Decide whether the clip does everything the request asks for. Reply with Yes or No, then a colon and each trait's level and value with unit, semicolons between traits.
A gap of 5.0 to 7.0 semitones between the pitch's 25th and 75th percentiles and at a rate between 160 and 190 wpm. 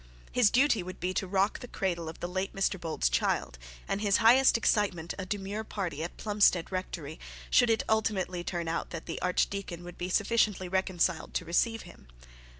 No: average, 3.2 semitones; average, 180 wpm